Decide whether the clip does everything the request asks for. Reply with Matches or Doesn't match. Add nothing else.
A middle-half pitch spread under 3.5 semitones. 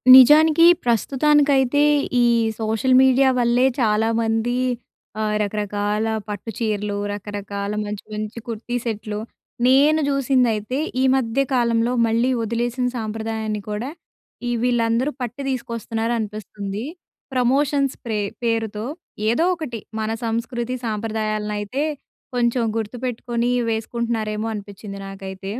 Matches